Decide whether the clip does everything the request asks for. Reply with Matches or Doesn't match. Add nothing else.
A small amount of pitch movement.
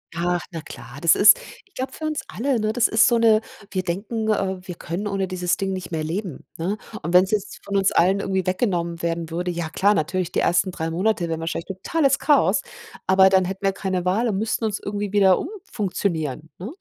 Doesn't match